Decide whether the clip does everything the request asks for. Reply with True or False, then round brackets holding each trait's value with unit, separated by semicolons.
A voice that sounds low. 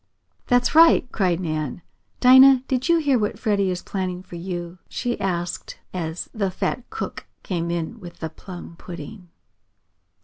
False (185 Hz)